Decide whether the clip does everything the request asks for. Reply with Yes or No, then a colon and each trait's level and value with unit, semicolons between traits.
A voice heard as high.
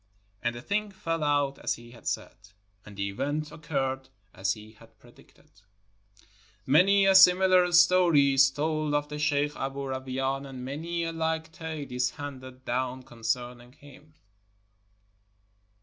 No: medium, 140 Hz